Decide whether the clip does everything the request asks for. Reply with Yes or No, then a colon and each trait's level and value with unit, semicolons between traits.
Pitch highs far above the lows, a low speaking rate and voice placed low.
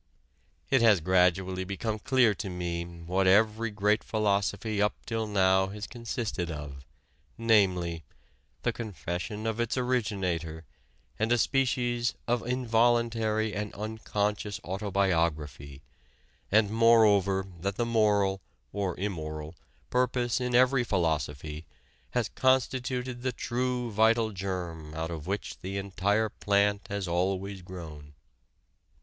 No: average, 4.1 semitones; slow, 120 wpm; low, 100 Hz